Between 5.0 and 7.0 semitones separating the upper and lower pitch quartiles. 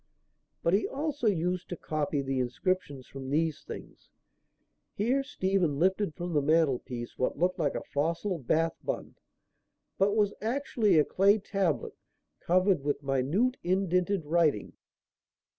Yes: average, 5.3 semitones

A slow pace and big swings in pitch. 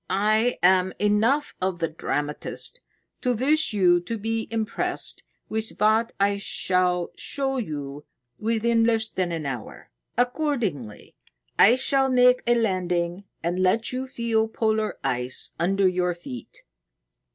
No: slow, 130 wpm; average, 4.7 semitones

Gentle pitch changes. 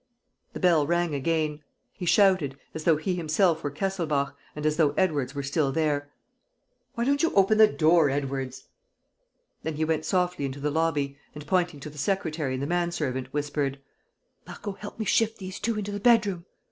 No: average, 4.5 semitones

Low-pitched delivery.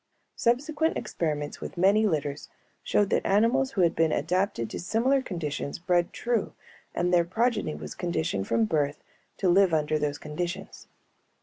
No: medium, 175 Hz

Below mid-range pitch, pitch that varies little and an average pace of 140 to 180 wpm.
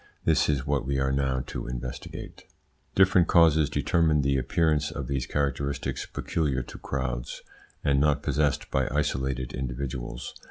Yes: very low, 70 Hz; narrow, 2.3 semitones; average, 145 wpm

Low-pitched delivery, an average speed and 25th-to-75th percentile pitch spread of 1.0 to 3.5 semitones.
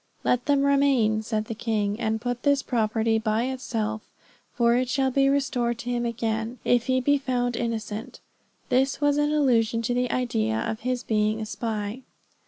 No: high, 235 Hz; average, 180 wpm; average, 2.7 semitones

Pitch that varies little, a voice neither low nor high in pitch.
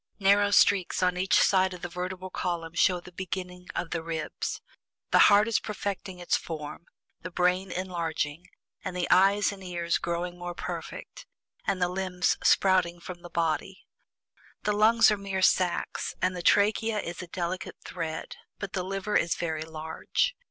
Yes: narrow, 2.0 semitones; medium, 180 Hz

